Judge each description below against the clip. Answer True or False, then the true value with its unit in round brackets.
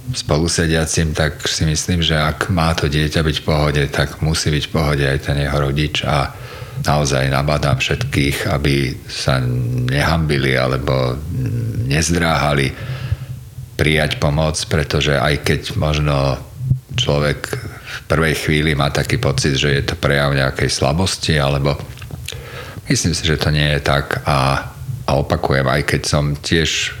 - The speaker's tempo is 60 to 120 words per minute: False (140 wpm)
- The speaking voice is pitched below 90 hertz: True (75 Hz)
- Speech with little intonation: False (3.1 semitones)